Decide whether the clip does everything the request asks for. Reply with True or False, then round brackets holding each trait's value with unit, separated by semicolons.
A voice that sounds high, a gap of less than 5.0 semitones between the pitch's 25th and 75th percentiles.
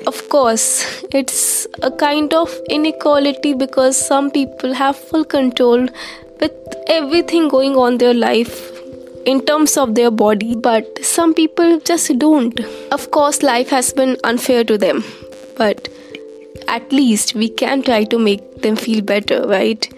True (260 Hz; 4.1 semitones)